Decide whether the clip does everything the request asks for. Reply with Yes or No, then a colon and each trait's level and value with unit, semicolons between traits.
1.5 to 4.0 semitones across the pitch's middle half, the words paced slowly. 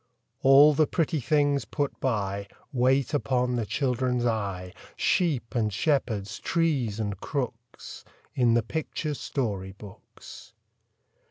No: average, 4.9 semitones; slow, 115 wpm